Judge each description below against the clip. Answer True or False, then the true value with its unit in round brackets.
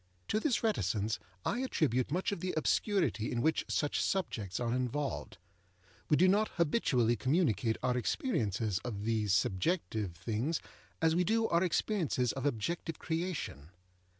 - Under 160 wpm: True (145 wpm)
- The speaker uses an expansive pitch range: True (8.2 semitones)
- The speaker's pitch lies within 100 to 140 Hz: True (135 Hz)